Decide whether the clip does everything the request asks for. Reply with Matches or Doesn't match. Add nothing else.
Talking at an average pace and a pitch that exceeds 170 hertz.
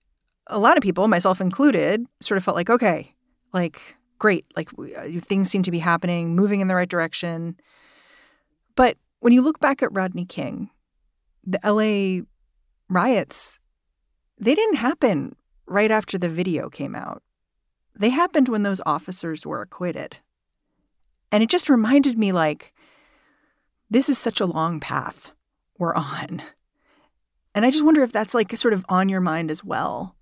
Matches